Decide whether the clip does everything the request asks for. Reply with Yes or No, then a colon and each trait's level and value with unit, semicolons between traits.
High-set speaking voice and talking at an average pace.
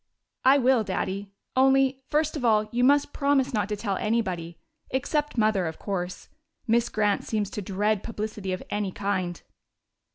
Yes: high, 215 Hz; average, 160 wpm